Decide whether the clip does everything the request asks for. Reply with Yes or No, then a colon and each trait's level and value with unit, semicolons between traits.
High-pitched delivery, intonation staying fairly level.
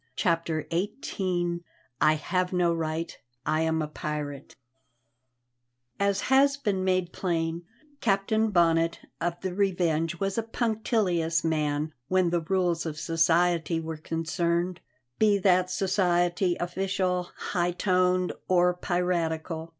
No: medium, 175 Hz; narrow, 2.3 semitones